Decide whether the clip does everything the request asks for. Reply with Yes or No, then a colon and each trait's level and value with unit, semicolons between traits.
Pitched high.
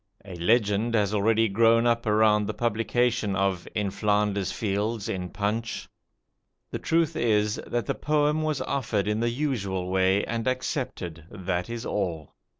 No: low, 105 Hz